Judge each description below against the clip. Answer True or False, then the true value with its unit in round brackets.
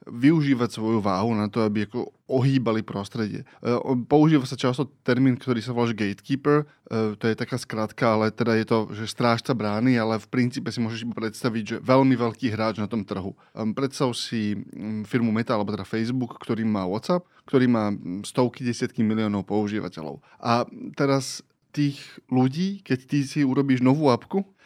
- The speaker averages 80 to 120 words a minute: False (165 wpm)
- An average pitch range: True (3.2 semitones)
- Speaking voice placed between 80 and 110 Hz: False (120 Hz)